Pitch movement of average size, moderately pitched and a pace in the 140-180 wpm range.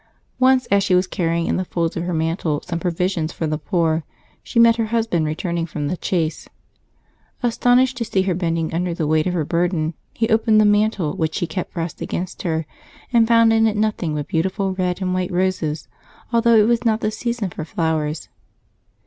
No: average, 4.8 semitones; medium, 180 Hz; average, 200 wpm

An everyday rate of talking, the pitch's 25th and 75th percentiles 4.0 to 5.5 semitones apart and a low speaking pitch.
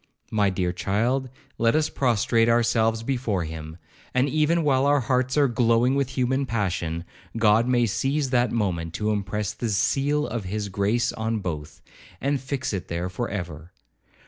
Yes: average, 165 wpm; average, 4.9 semitones; low, 115 Hz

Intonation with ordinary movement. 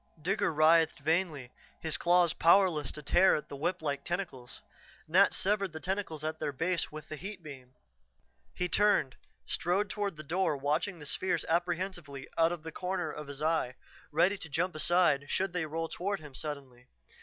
Yes: average, 3.5 semitones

